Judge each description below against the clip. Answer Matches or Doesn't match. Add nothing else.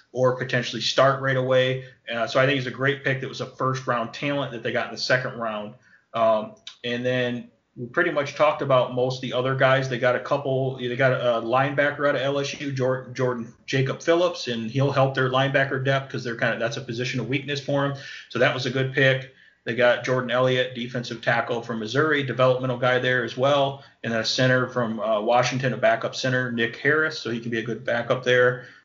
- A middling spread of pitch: Doesn't match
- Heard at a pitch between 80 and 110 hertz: Doesn't match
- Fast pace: Matches